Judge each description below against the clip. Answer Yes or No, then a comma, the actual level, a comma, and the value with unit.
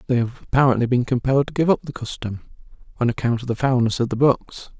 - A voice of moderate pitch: No, low, 125 Hz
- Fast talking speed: Yes, fast, 225 wpm